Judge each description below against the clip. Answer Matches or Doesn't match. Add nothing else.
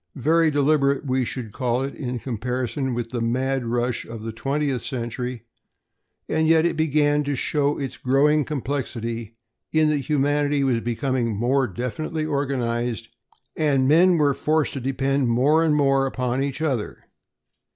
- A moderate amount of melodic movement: Matches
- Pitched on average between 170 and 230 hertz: Doesn't match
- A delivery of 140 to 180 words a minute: Matches